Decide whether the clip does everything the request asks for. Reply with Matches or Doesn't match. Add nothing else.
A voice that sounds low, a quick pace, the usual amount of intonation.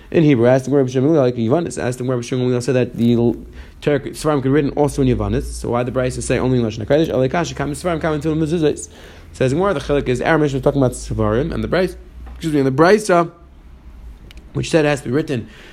Doesn't match